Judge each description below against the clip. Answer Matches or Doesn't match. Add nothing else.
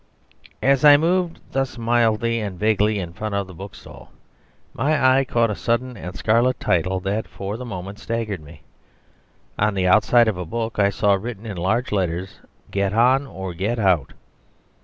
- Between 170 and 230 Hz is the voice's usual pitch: Doesn't match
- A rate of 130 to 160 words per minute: Doesn't match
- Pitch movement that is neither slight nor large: Matches